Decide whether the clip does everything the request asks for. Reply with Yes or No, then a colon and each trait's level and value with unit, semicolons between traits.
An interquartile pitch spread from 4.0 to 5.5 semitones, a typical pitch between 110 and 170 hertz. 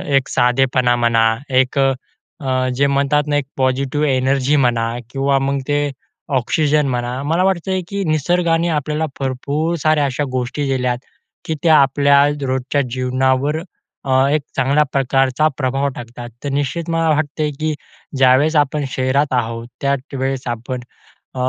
No: narrow, 2.6 semitones; low, 135 Hz